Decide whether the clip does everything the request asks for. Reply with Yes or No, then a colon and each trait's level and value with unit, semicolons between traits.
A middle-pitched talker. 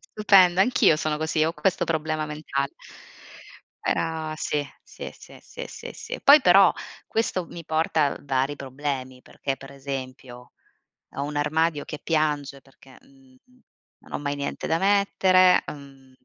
Yes: medium, 155 Hz